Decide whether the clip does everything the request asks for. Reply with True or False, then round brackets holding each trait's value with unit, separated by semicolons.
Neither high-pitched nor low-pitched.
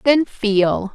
False (225 Hz)